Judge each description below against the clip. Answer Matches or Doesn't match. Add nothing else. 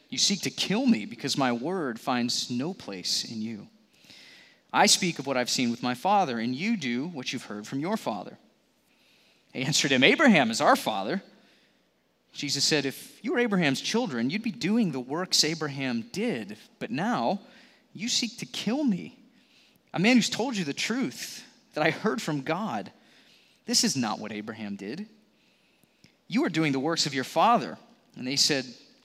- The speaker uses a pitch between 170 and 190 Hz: Matches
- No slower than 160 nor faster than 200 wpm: Matches